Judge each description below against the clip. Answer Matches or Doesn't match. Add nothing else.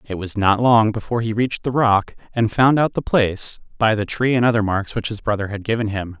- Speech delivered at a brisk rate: Matches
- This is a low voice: Matches